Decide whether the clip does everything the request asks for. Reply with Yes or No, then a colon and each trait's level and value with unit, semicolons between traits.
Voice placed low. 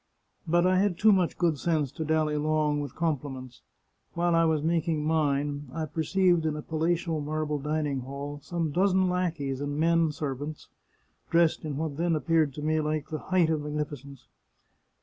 No: medium, 155 Hz